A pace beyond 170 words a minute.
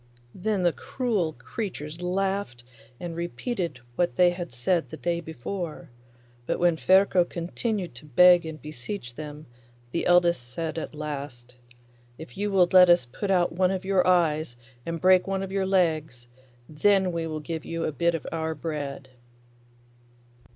No: average, 160 wpm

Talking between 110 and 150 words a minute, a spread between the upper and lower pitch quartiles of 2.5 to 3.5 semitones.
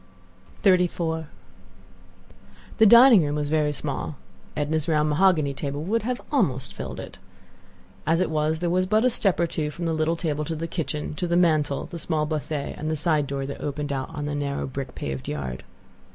No: average, 190 wpm; average, 2.9 semitones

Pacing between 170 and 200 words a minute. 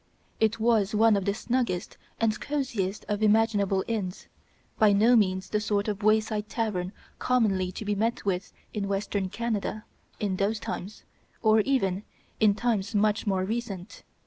No: average, 155 wpm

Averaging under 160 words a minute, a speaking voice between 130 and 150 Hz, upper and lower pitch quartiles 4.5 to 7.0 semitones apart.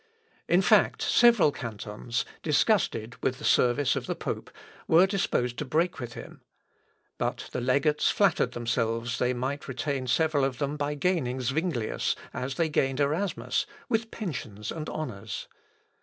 Yes: average, 145 wpm; medium, 140 Hz; average, 4.8 semitones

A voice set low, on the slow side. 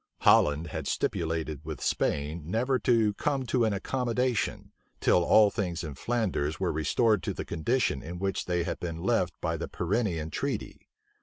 No: very low, 90 Hz; average, 165 wpm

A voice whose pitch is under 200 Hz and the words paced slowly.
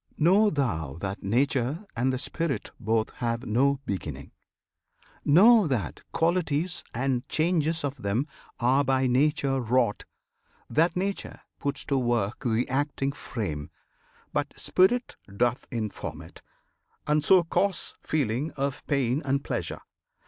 Yes: low, 135 Hz; slow, 125 wpm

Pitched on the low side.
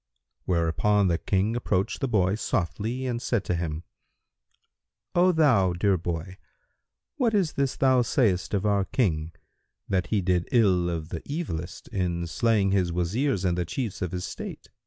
Yes: very low, 95 Hz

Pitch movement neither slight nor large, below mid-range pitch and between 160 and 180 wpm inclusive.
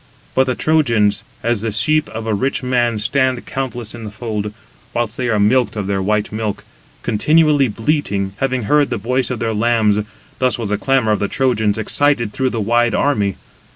No: average, 3.6 semitones; low, 115 Hz; average, 190 wpm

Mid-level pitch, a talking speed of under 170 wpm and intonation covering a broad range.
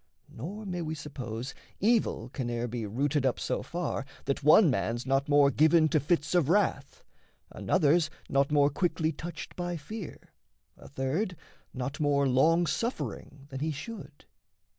No: medium, 150 Hz; average, 155 wpm; average, 4.2 semitones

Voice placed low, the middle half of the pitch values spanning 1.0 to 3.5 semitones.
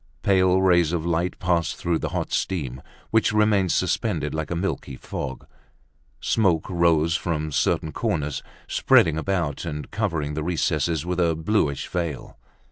Yes: very low, 85 Hz; average, 3.0 semitones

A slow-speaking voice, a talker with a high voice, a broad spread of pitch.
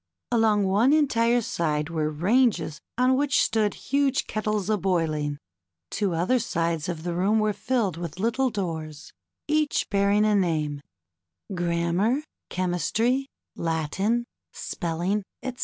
Yes: slow, 125 wpm; high, 200 Hz; wide, 5.7 semitones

